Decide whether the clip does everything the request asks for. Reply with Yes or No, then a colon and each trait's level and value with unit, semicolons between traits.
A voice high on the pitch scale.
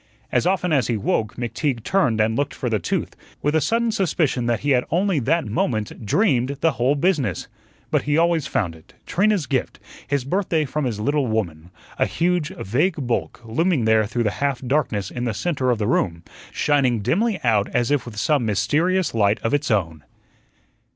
No: low, 130 Hz